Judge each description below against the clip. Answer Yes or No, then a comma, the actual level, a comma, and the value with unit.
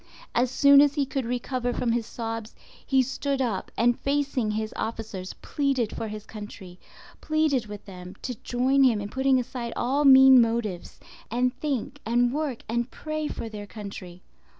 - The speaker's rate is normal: Yes, average, 165 wpm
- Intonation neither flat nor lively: Yes, average, 3.7 semitones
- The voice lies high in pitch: Yes, high, 240 Hz